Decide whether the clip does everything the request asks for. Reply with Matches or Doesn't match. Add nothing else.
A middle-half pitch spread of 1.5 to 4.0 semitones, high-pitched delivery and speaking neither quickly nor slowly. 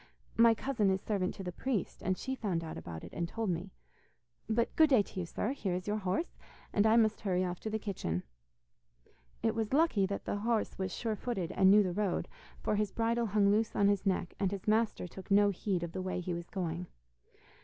Doesn't match